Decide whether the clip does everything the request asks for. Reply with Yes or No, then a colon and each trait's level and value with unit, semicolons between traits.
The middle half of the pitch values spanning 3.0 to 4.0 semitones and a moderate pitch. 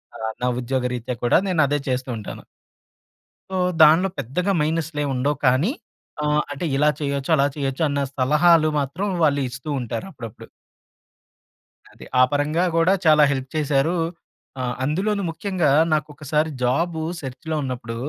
Yes: average, 3.5 semitones; medium, 145 Hz